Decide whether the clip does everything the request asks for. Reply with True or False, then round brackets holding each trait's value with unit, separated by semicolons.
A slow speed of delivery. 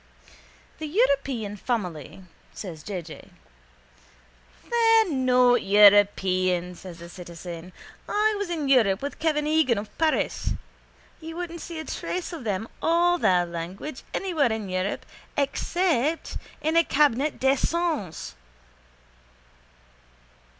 True (115 wpm)